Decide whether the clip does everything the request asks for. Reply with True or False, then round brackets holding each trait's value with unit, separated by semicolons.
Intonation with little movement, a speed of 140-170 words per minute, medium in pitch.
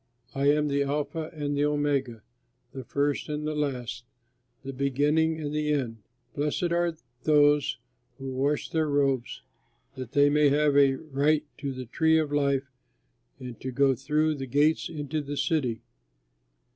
True (1.9 semitones; 160 wpm; 145 Hz)